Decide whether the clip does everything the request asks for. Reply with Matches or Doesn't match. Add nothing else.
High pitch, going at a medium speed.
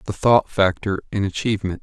Doesn't match